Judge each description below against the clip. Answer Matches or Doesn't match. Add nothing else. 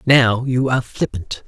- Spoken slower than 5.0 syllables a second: Matches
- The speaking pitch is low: Matches